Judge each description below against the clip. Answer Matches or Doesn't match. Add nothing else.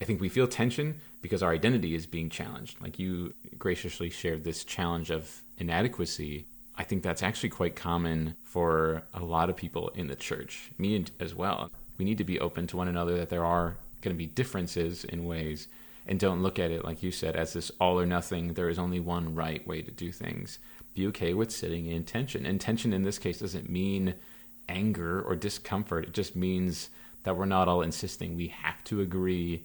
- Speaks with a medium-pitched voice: Doesn't match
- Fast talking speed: Matches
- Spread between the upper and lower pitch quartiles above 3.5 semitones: Doesn't match